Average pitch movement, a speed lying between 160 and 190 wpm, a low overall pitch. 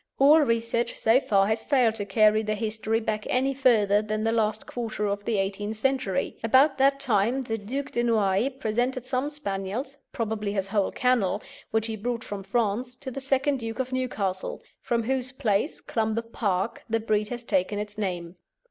No: average, 3.5 semitones; average, 185 wpm; high, 225 Hz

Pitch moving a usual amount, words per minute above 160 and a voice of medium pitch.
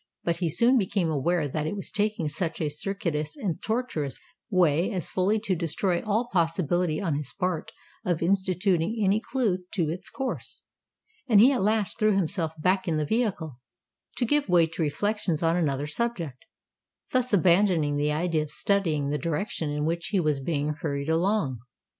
Yes: average, 4.8 semitones; average, 170 wpm; medium, 175 Hz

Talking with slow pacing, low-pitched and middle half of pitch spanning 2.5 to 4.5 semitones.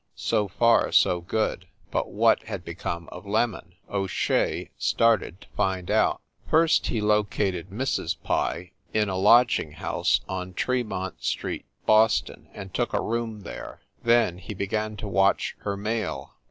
No: average, 150 wpm; low, 105 Hz; average, 3.2 semitones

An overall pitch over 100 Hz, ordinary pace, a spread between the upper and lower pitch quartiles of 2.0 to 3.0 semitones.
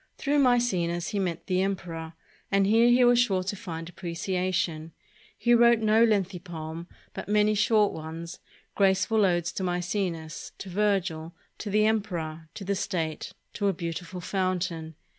No: medium, 185 Hz; average, 155 wpm; average, 3.7 semitones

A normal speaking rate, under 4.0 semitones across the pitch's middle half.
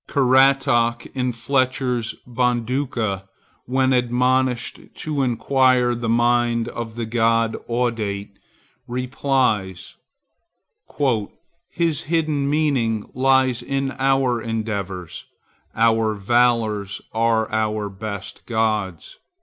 No: slow, 85 wpm; average, 2.8 semitones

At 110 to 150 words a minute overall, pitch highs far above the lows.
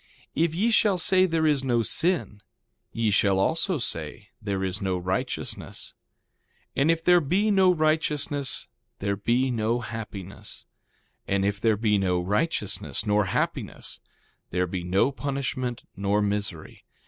Yes: average, 140 wpm; wide, 7.8 semitones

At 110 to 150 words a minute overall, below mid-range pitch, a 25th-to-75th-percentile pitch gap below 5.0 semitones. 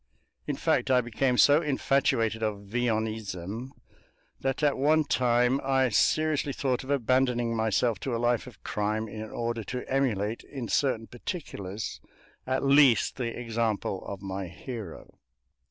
Yes: average, 140 wpm; low, 120 Hz; average, 3.4 semitones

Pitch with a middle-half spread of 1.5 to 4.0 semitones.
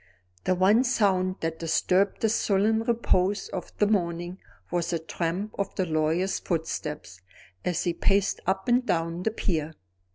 Yes: average, 3.4 semitones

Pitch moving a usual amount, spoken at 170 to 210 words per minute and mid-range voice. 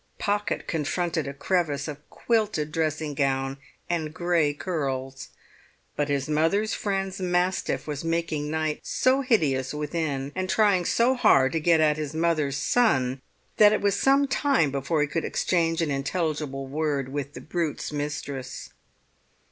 No: average, 4.0 semitones; average, 150 wpm; medium, 155 Hz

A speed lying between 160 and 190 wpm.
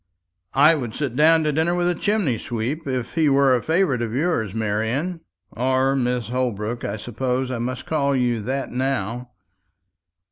Yes: average, 170 wpm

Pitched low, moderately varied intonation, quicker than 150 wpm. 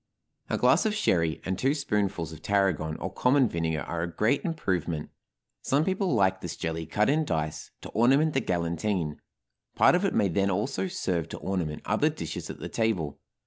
No: very low, 95 Hz; wide, 8.5 semitones; average, 185 wpm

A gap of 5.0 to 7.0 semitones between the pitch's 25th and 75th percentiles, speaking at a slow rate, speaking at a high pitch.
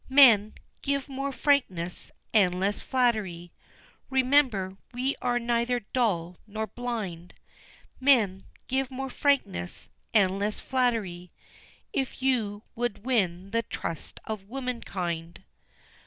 Yes: average, 5.3 semitones; slow, 110 wpm; high, 225 Hz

